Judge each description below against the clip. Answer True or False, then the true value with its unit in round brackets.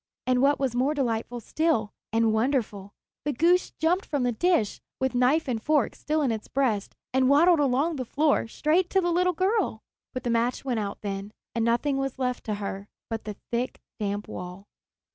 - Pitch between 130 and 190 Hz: False (255 Hz)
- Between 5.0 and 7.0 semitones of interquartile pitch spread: True (5.3 semitones)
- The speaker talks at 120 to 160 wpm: False (195 wpm)